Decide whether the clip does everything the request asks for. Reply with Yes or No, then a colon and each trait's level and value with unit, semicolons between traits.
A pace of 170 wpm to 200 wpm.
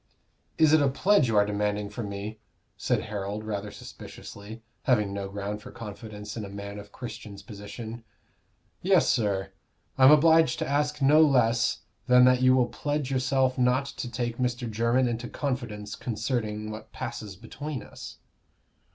No: average, 160 wpm